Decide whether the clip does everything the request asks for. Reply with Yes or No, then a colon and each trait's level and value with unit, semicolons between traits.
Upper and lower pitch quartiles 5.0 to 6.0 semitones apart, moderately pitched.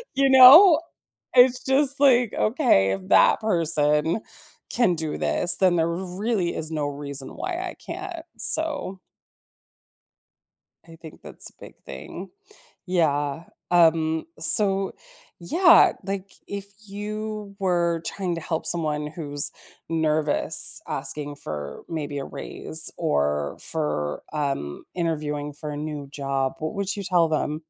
Yes: wide, 5.4 semitones; medium, 165 Hz